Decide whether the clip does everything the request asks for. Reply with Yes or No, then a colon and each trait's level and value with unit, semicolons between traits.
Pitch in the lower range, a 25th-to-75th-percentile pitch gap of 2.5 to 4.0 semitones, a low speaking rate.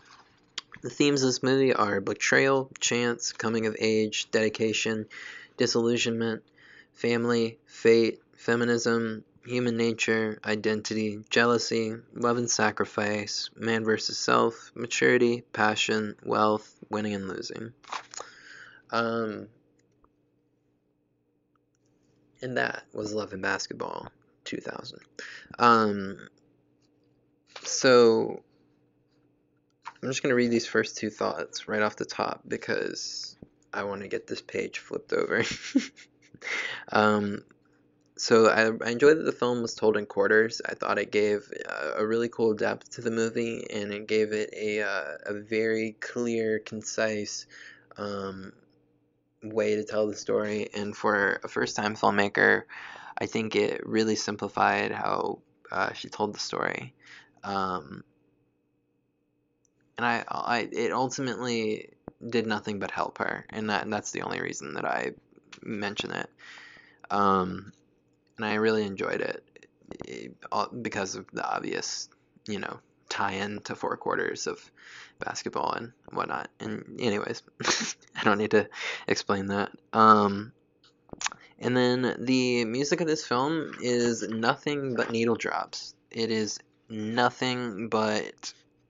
Yes: low, 110 Hz; average, 3.3 semitones; slow, 130 wpm